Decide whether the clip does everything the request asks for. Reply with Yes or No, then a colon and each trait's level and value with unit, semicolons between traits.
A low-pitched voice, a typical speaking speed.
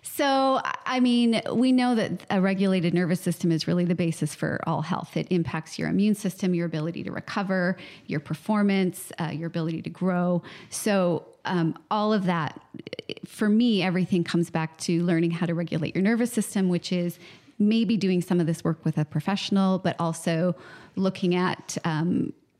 No: medium, 180 Hz; average, 180 wpm